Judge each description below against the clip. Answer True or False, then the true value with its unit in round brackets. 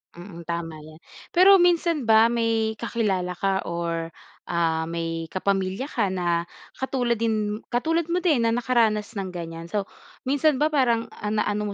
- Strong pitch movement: True (5.9 semitones)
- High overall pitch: True (210 Hz)